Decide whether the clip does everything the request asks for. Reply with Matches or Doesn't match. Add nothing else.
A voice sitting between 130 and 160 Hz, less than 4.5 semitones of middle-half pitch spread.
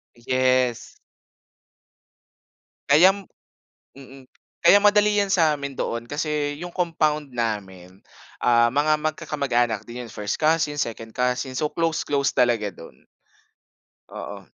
Doesn't match